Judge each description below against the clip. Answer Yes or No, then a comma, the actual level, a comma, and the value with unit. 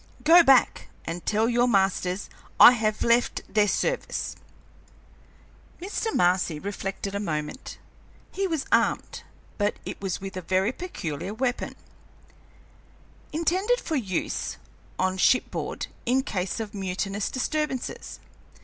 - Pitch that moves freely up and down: Yes, wide, 5.9 semitones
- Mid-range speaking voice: No, high, 210 Hz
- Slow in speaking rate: Yes, slow, 120 wpm